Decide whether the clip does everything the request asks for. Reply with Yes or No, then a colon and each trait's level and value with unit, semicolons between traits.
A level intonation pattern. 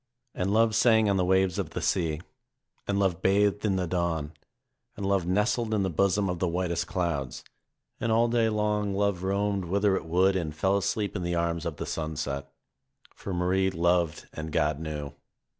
No: average, 3.2 semitones